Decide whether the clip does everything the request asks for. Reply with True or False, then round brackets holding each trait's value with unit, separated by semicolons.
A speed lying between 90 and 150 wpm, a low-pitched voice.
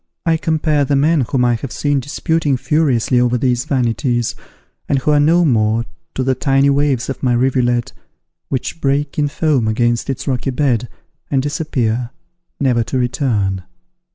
False (160 wpm; 130 Hz)